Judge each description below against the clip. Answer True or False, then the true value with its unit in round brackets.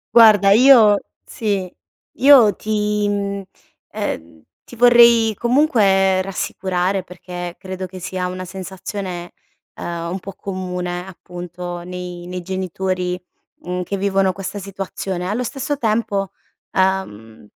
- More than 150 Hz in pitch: True (190 Hz)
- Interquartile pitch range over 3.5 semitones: False (2.5 semitones)